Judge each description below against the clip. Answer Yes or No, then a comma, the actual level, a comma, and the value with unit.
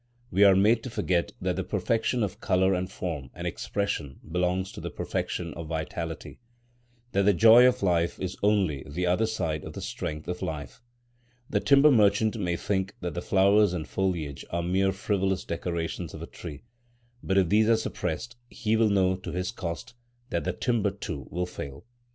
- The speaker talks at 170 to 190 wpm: Yes, average, 185 wpm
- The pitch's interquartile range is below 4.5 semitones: Yes, average, 3.8 semitones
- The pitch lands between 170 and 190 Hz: No, very low, 95 Hz